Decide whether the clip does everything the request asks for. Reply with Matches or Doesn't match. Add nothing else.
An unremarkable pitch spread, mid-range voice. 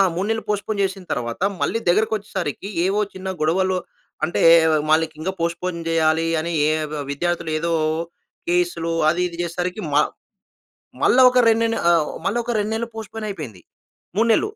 Matches